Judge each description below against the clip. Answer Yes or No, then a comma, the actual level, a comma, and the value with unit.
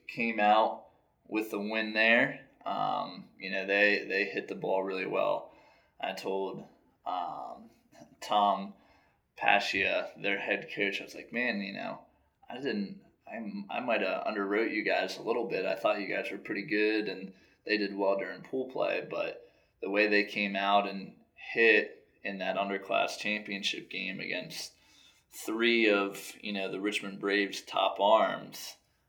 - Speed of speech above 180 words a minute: No, average, 165 wpm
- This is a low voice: Yes, low, 105 Hz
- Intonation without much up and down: Yes, narrow, 2.0 semitones